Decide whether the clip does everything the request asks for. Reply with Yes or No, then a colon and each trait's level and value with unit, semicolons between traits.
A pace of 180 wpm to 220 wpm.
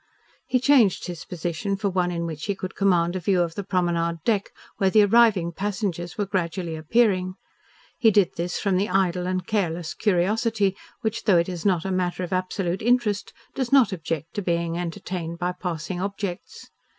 Yes: average, 185 wpm